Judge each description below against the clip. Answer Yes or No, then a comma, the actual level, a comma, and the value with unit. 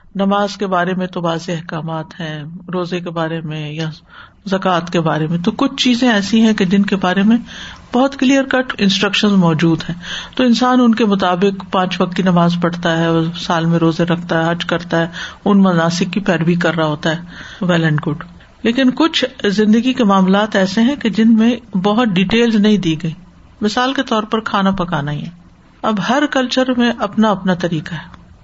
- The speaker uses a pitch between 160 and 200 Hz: Yes, high, 190 Hz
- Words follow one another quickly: Yes, fast, 200 wpm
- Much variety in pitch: No, average, 5.0 semitones